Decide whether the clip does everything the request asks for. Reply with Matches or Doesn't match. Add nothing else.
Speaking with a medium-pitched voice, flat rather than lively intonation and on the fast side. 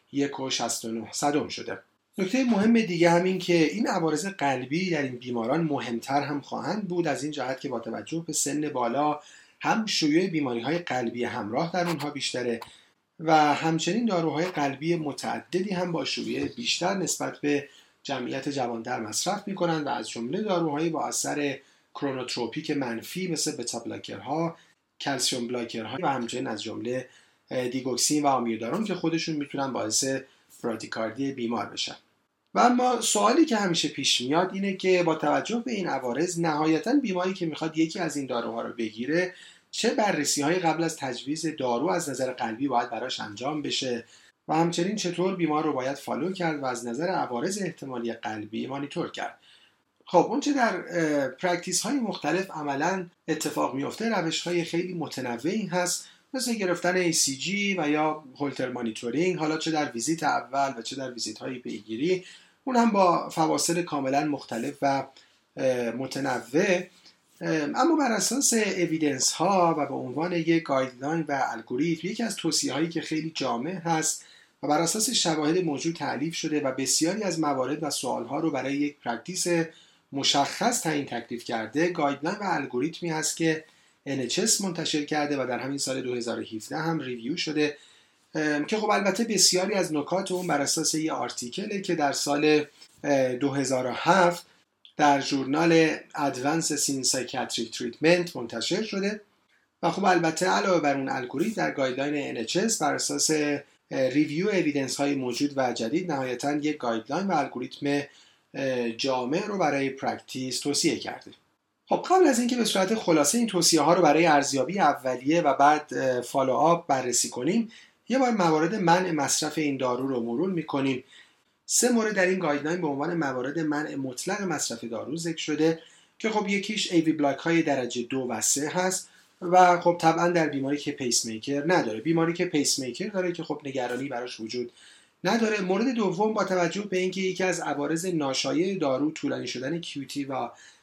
Doesn't match